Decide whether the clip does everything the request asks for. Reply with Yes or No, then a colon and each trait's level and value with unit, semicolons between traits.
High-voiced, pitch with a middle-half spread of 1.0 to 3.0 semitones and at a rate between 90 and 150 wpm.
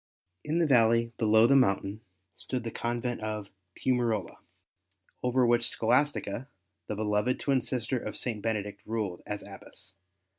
No: low, 115 Hz; average, 2.7 semitones; average, 140 wpm